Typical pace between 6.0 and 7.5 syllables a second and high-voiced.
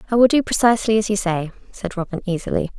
Yes: 7.0 syllables/s; high, 205 Hz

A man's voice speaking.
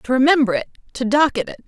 No: female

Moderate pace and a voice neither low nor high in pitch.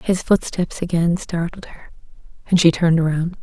Yes: average, 160 wpm; medium, 170 Hz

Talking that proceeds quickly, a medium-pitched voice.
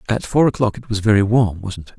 No: fast, 240 wpm; low, 105 Hz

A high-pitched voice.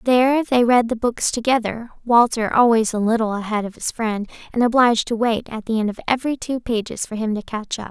Yes: high, 230 Hz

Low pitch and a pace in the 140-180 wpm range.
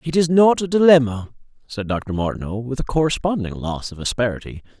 Yes: low, 130 Hz; average, 175 wpm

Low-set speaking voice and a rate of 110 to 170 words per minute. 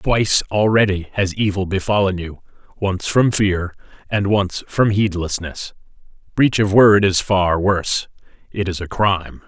Yes: very low, 95 Hz; average, 140 wpm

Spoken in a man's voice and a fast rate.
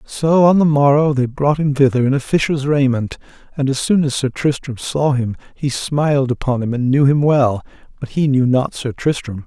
Yes: male; fast, 215 wpm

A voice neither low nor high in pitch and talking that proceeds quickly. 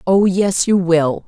No: medium, 180 Hz; average, 190 wpm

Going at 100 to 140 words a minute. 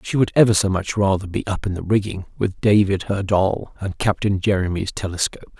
No: fast, 205 wpm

